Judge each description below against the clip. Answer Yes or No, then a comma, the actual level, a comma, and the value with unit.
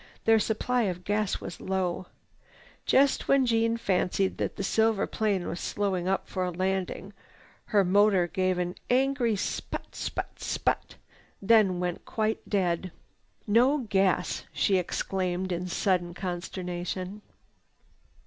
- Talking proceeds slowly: Yes, slow, 130 wpm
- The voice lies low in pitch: No, high, 190 Hz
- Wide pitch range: No, average, 3.1 semitones